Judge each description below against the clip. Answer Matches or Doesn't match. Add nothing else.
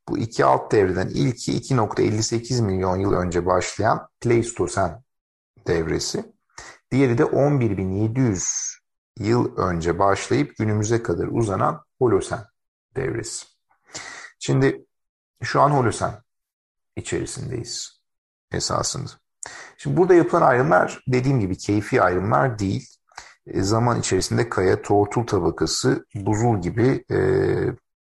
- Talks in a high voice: Doesn't match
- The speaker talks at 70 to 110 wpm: Matches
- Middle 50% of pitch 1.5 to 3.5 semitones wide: Doesn't match